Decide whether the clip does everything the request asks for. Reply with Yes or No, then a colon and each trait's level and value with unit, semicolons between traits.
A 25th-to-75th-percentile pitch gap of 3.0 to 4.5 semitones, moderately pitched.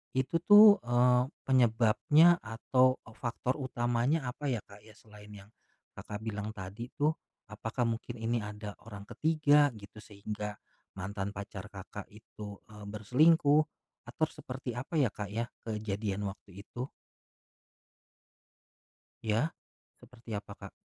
No: average, 3.9 semitones; low, 115 Hz